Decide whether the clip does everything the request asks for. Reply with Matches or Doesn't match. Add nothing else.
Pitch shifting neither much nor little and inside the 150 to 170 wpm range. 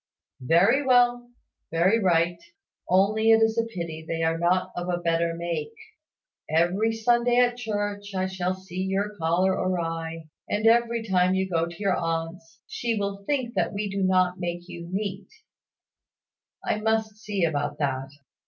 Matches